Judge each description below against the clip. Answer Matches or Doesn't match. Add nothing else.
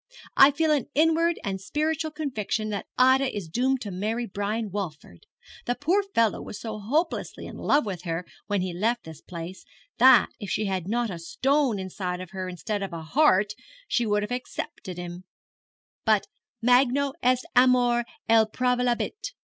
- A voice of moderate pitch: Doesn't match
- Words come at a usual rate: Matches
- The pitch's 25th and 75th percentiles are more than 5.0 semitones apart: Matches